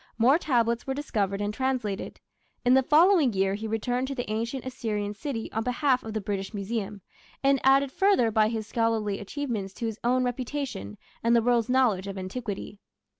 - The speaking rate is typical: Yes, average, 180 wpm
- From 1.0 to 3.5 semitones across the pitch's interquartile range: No, average, 3.9 semitones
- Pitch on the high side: Yes, high, 230 Hz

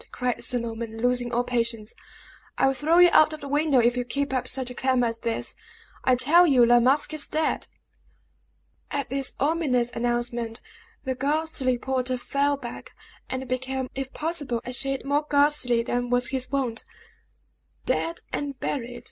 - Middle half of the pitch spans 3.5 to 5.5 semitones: No, average, 2.7 semitones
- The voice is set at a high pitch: Yes, very high, 255 Hz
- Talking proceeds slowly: No, average, 170 wpm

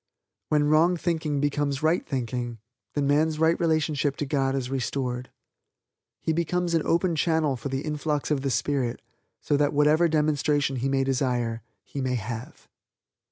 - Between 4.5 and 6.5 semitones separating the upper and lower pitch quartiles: No, average, 2.8 semitones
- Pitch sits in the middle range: Yes, medium, 145 Hz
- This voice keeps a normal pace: Yes, average, 160 wpm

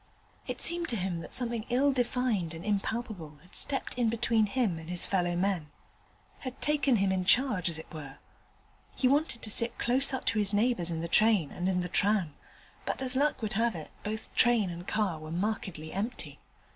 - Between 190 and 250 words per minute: Yes, average, 200 wpm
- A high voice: Yes, high, 210 Hz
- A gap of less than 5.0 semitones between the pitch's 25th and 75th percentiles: No, wide, 5.5 semitones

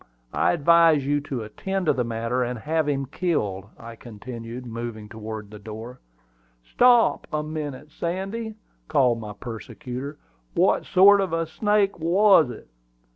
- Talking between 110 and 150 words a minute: Yes, average, 145 wpm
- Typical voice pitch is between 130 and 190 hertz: Yes, medium, 140 Hz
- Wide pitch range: Yes, wide, 6.6 semitones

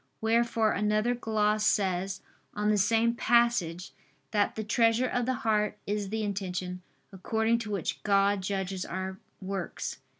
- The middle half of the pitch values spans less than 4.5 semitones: Yes, average, 2.7 semitones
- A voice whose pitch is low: No, high, 210 Hz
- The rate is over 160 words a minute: No, average, 140 wpm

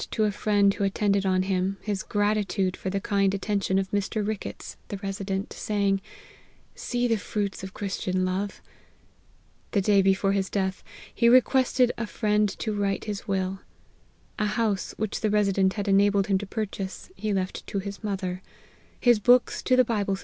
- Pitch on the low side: No, high, 200 Hz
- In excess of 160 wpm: Yes, average, 180 wpm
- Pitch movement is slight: Yes, narrow, 1.6 semitones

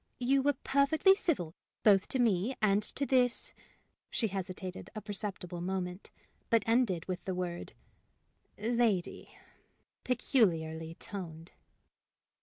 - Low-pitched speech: No, high, 200 Hz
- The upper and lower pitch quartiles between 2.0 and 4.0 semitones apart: No, wide, 5.5 semitones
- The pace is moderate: No, slow, 115 wpm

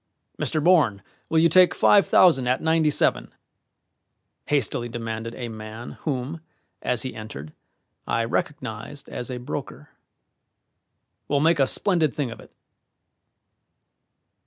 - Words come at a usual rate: No, slow, 125 wpm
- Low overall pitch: Yes, low, 130 Hz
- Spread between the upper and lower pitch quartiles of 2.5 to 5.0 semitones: No, wide, 5.4 semitones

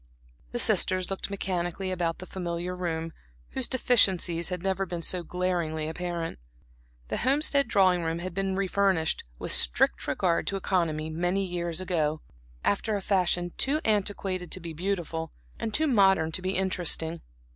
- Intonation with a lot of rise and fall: No, narrow, 2.5 semitones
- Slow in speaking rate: No, average, 155 wpm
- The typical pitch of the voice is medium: Yes, medium, 180 Hz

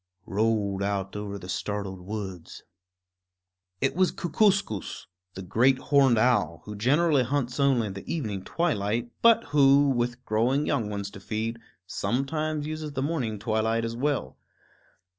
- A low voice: Yes, low, 115 Hz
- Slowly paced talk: No, average, 145 wpm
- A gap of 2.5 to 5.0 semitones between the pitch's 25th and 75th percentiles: No, wide, 5.6 semitones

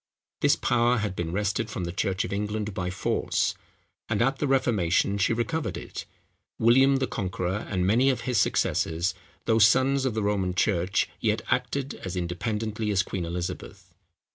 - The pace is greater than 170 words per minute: No, average, 165 wpm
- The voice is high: No, low, 105 Hz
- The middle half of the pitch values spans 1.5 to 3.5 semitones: No, average, 4.5 semitones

